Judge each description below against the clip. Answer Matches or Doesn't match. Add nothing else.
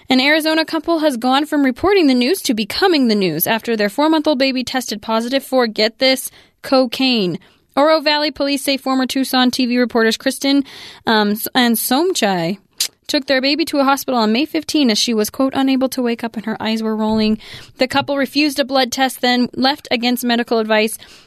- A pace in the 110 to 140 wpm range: Doesn't match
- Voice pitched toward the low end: Doesn't match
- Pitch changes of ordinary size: Matches